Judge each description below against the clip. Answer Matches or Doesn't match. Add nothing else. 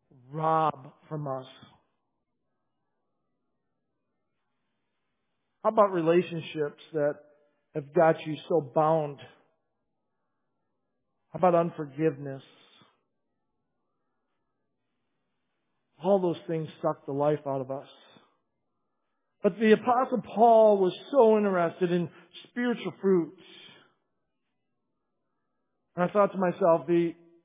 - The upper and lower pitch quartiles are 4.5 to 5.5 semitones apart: Doesn't match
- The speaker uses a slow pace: Matches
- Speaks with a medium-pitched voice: Matches